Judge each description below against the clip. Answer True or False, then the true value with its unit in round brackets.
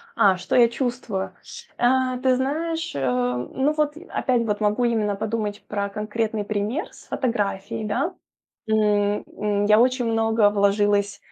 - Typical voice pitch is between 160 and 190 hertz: False (215 Hz)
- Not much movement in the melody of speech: False (3.6 semitones)